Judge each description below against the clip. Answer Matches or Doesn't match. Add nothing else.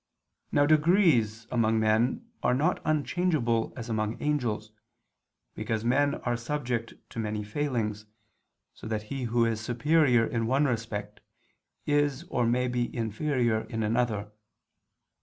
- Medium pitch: Doesn't match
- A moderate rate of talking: Doesn't match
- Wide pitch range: Doesn't match